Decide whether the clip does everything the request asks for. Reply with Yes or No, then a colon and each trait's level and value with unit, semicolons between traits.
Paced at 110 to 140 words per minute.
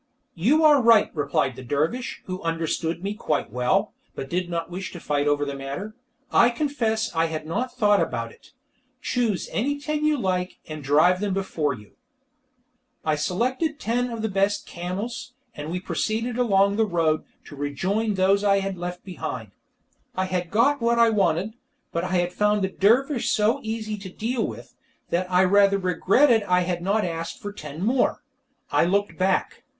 No: average, 175 wpm